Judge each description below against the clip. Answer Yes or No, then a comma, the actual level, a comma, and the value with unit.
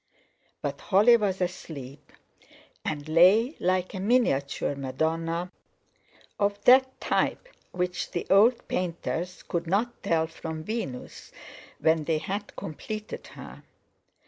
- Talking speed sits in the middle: No, slow, 115 wpm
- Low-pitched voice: No, medium, 180 Hz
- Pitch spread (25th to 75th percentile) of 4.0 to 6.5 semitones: Yes, average, 4.4 semitones